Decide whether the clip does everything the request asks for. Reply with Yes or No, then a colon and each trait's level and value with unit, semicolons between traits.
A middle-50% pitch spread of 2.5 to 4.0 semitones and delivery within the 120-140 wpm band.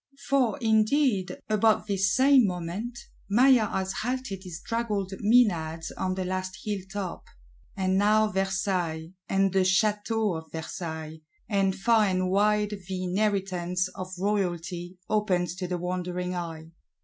Yes: average, 2.9 semitones; slow, 135 wpm